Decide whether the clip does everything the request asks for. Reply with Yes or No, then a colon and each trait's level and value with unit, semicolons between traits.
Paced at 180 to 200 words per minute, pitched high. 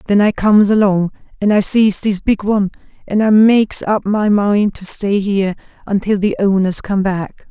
Yes: average, 190 wpm; high, 200 Hz